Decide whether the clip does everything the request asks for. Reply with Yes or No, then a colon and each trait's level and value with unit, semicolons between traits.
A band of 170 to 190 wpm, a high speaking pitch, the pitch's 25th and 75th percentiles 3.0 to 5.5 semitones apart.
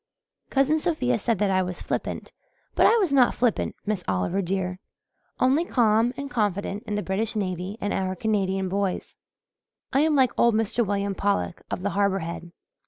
Yes: average, 175 wpm; high, 205 Hz; average, 4.3 semitones